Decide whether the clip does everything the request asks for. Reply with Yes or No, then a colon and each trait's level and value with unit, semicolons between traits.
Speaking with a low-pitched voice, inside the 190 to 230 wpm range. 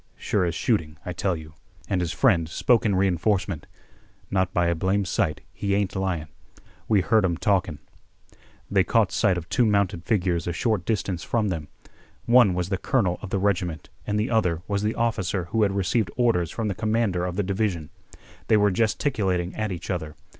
Yes: very low, 95 Hz; average, 195 wpm